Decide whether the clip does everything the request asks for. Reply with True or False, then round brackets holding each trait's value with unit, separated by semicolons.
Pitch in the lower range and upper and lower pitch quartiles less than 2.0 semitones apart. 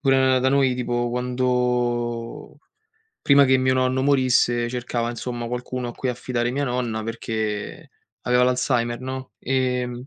True (125 Hz; 1.3 semitones)